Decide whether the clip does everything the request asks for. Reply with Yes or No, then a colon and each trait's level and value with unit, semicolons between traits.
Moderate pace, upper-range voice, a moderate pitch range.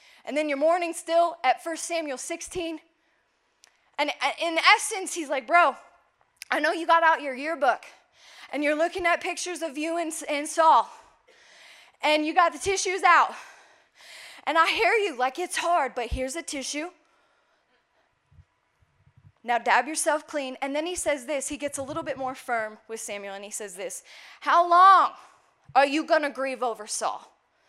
Yes: average, 170 wpm; very high, 320 Hz; average, 3.5 semitones